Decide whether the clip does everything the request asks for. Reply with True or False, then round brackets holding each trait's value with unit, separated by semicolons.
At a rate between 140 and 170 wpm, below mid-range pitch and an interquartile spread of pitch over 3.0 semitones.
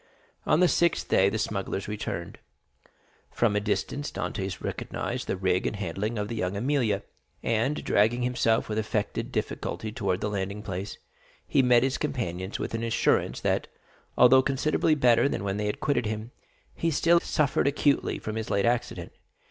True (165 wpm; 110 Hz; 4.1 semitones)